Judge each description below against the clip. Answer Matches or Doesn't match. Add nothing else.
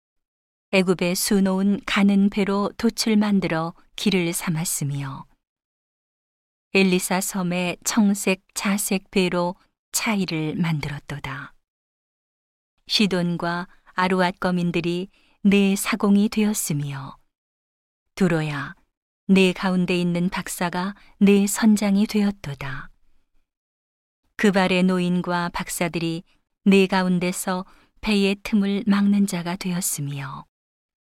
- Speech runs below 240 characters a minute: Matches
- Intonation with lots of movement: Doesn't match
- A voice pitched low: Doesn't match